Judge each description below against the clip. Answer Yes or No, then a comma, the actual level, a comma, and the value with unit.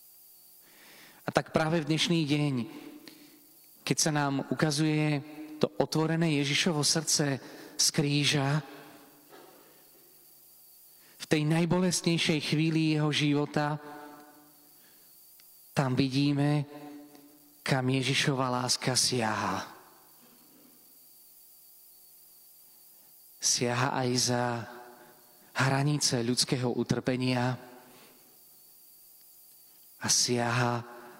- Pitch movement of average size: Yes, average, 3.2 semitones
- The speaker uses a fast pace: No, slow, 70 wpm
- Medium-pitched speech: Yes, medium, 145 Hz